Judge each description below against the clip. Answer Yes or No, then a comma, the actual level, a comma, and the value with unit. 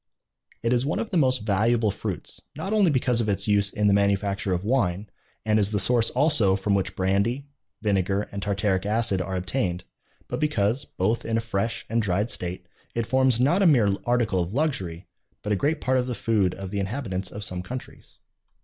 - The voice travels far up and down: No, average, 4.1 semitones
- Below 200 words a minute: No, fast, 205 wpm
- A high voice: No, low, 105 Hz